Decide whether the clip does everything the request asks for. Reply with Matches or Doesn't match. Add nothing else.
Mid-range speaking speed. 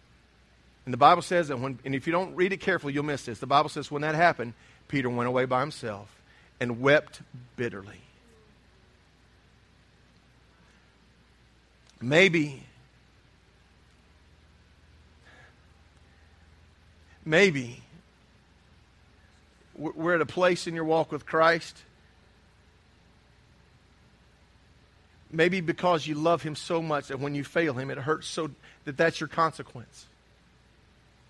Doesn't match